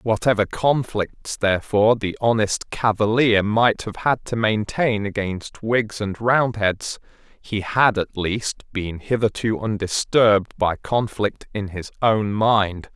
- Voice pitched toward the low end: Yes, low, 105 Hz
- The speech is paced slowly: Yes, slow, 130 wpm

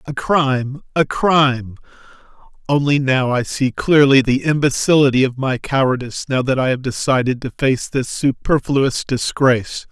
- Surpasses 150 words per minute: No, average, 145 wpm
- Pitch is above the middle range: No, low, 135 Hz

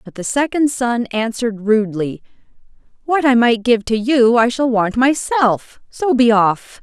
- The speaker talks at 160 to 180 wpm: Yes, average, 165 wpm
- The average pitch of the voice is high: Yes, high, 235 Hz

